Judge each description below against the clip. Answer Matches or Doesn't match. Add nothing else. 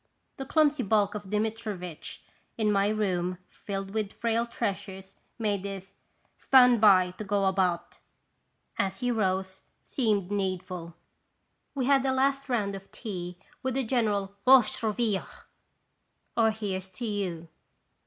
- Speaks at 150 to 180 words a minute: Doesn't match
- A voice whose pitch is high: Matches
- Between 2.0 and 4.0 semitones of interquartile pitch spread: Matches